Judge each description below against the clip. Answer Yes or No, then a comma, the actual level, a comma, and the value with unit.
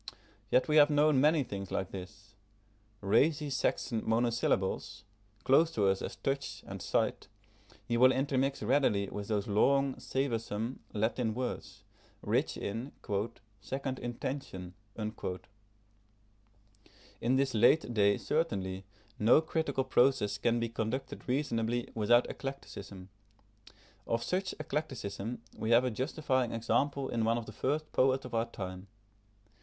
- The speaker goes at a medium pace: No, slow, 130 wpm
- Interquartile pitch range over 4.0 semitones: Yes, average, 4.6 semitones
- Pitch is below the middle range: Yes, low, 115 Hz